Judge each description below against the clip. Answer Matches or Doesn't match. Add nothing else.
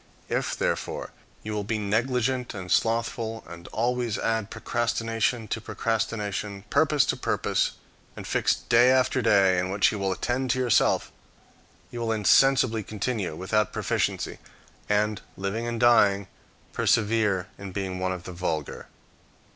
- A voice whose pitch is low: Matches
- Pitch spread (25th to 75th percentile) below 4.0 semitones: Matches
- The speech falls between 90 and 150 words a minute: Matches